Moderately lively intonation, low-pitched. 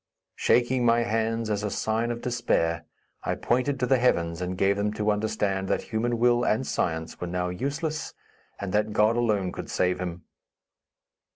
Yes: average, 4.5 semitones; low, 110 Hz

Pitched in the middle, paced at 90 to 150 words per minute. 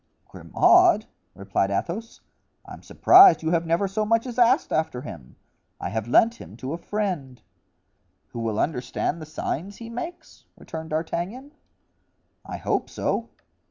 Yes: medium, 170 Hz; average, 145 wpm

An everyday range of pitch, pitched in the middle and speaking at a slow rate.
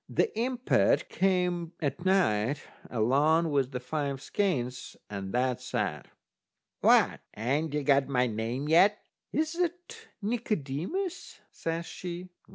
No: wide, 6.9 semitones; medium, 155 Hz; slow, 120 wpm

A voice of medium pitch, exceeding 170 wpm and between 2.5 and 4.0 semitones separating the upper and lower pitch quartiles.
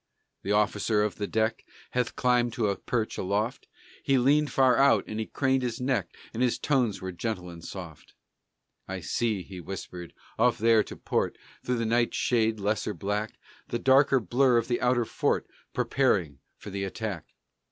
No: low, 110 Hz; average, 180 wpm; average, 3.7 semitones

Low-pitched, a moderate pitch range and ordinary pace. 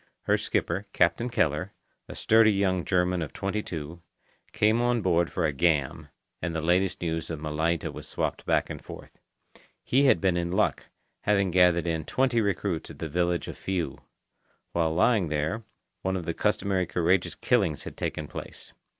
Yes: very low, 90 Hz; average, 3.2 semitones; average, 175 wpm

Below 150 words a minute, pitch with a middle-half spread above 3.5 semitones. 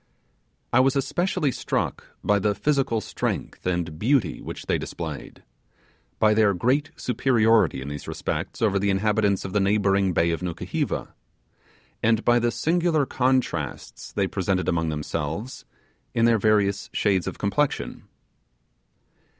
Yes: slow, 135 wpm; average, 4.8 semitones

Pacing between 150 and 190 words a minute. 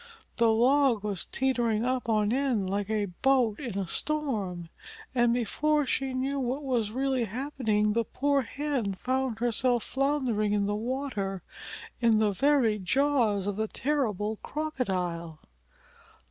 No: average, 140 wpm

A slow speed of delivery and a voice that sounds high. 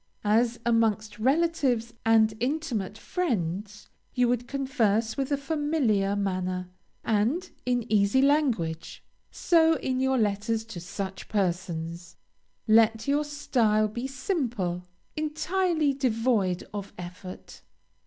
Yes: slow, 110 wpm; high, 225 Hz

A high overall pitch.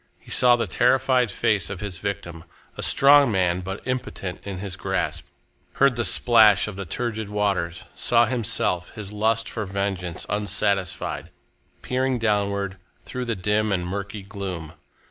No: low, 105 Hz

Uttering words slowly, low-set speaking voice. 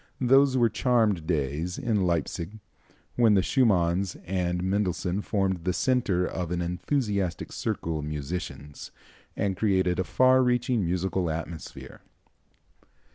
Yes: slow, 125 wpm; very low, 95 Hz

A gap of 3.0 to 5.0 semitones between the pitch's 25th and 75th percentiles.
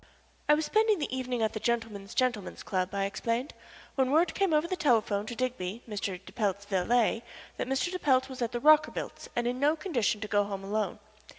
No: wide, 5.4 semitones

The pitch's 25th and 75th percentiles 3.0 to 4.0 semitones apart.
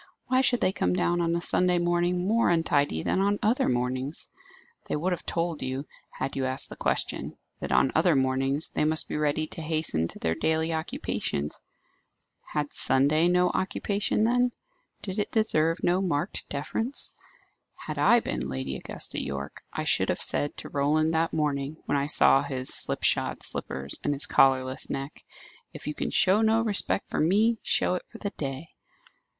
No: average, 5.0 semitones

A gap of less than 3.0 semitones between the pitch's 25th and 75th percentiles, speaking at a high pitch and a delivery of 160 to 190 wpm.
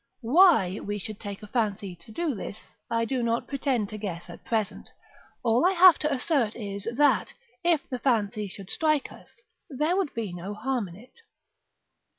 No: wide, 5.6 semitones; high, 230 Hz; average, 180 wpm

